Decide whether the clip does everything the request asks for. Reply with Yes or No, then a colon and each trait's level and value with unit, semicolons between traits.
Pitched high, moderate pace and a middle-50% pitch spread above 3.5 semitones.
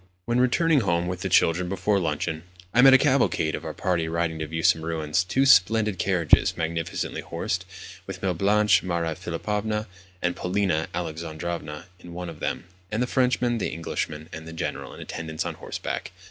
No: very low, 90 Hz; average, 180 wpm; average, 4.3 semitones